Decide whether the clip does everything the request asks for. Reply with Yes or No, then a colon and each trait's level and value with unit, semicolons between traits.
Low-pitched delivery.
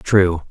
Yes: very low, 90 Hz